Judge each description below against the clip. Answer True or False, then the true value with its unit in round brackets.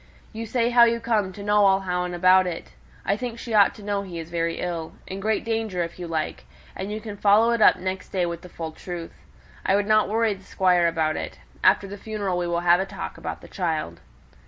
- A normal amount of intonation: True (3.5 semitones)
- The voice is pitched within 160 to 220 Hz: True (190 Hz)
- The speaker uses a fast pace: True (240 wpm)